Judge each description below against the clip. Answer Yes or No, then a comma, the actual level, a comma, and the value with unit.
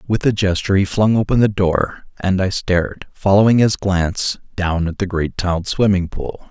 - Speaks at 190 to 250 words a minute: Yes, average, 195 wpm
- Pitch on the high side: No, very low, 95 Hz